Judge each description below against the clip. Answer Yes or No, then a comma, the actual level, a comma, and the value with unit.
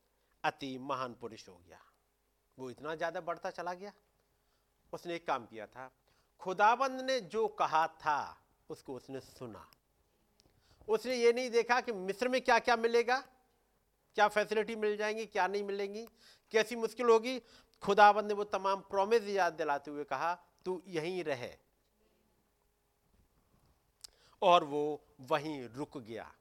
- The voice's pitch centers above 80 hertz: Yes, high, 190 Hz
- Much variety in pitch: Yes, wide, 6.9 semitones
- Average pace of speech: Yes, average, 140 wpm